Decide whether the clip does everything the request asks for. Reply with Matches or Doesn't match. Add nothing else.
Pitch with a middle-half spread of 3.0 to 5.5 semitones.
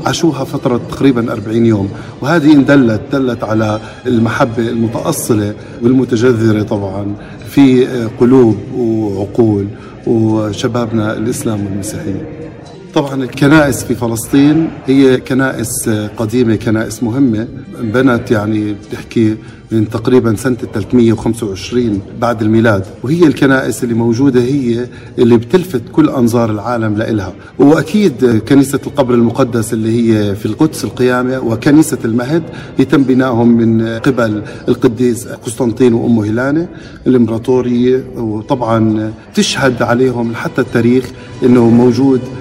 Doesn't match